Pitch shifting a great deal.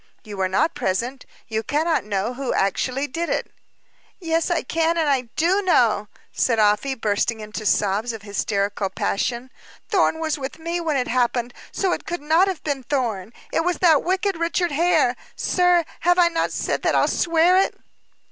Yes: wide, 7.2 semitones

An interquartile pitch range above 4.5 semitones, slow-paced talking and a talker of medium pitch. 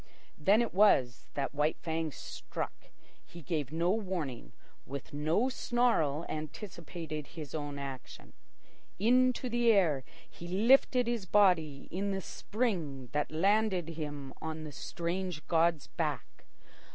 Yes: wide, 5.4 semitones; slow, 125 wpm; medium, 165 Hz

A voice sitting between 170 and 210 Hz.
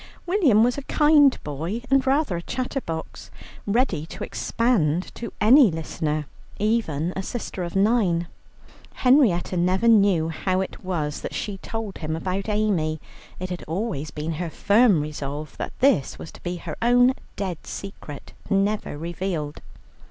Yes: high, 190 Hz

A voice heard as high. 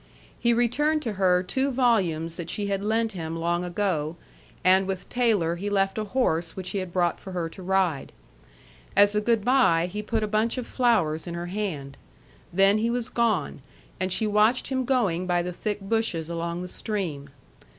Yes: high, 195 Hz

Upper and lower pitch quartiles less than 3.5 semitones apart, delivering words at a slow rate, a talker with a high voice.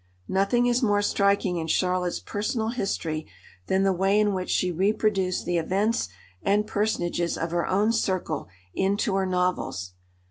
No: narrow, 2.6 semitones; average, 150 wpm; high, 195 Hz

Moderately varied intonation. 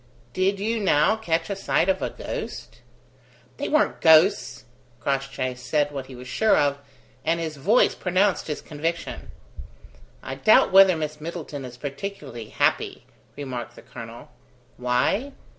No: wide, 6.0 semitones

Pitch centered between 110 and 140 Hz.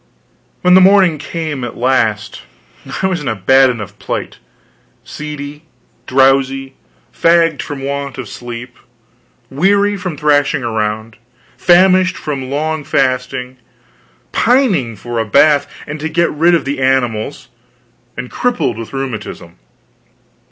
Yes: low, 135 Hz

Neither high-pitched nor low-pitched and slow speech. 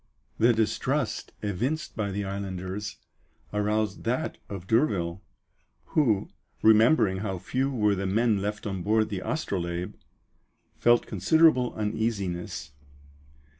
No: low, 105 Hz; slow, 110 wpm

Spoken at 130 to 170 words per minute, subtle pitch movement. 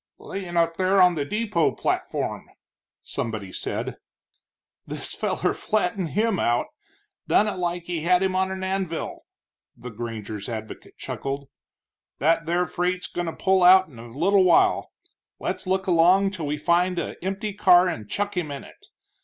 No: average, 160 wpm; average, 4.0 semitones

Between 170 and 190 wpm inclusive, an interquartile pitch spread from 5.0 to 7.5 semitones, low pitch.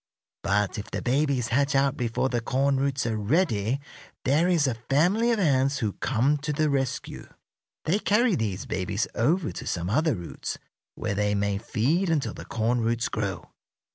Yes: average, 175 wpm; wide, 5.4 semitones; low, 130 Hz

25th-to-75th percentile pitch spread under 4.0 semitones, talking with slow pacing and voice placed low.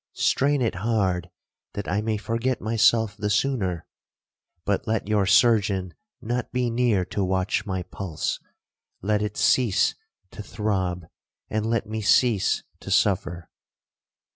Yes: average, 3.3 semitones; slow, 130 wpm; low, 105 Hz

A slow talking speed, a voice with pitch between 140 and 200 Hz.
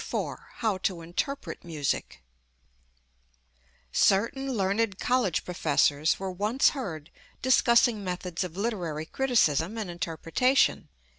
Yes: slow, 100 wpm; high, 190 Hz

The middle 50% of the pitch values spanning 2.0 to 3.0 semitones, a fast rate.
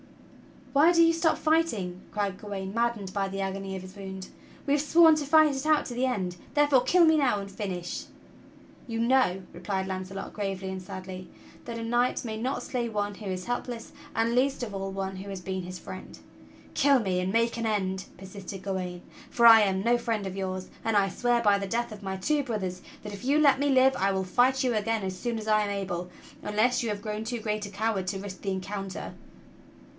No: average, 4.2 semitones; fast, 220 wpm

